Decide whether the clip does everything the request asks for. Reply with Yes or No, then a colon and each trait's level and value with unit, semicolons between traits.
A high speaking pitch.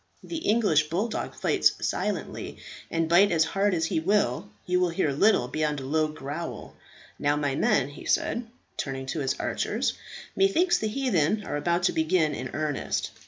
No: medium, 165 Hz